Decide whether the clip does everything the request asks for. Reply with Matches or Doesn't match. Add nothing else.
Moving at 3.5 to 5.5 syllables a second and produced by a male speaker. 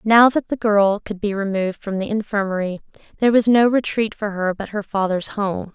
Doesn't match